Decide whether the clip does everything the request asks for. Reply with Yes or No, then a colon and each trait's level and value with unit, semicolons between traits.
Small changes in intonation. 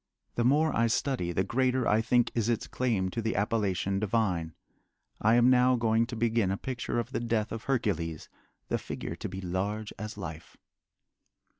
No: average, 3.6 semitones